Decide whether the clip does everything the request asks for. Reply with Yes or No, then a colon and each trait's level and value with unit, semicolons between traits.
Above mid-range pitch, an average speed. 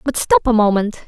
No: high, 235 Hz; fast, 225 wpm